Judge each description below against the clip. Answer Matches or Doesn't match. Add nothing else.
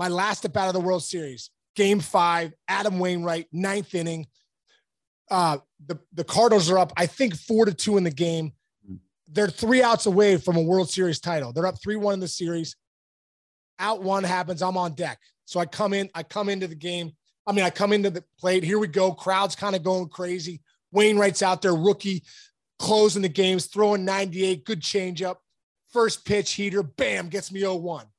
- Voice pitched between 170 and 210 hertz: Matches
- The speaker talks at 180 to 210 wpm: Matches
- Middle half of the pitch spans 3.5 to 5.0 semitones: Doesn't match